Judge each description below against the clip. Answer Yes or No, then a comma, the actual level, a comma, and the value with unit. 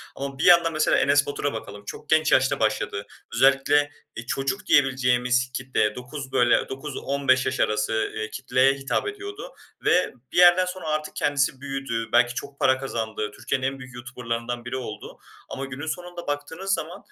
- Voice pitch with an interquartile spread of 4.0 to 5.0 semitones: No, average, 3.4 semitones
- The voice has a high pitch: No, low, 135 Hz